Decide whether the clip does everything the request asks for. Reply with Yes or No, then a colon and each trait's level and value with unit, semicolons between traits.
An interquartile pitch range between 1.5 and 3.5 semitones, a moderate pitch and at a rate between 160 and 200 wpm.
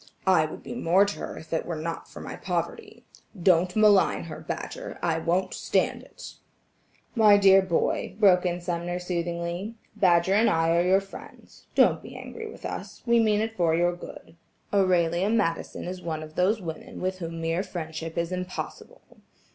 Yes: average, 3.0 semitones; medium, 180 Hz; average, 180 wpm